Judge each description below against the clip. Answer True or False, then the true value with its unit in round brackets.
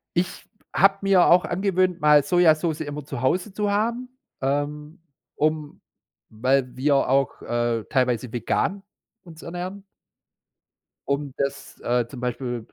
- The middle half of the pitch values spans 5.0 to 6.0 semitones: True (5.6 semitones)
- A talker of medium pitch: True (150 Hz)